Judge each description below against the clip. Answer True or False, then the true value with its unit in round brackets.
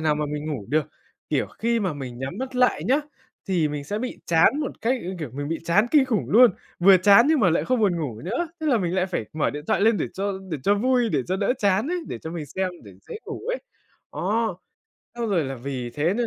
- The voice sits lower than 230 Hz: True (190 Hz)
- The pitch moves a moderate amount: False (7.6 semitones)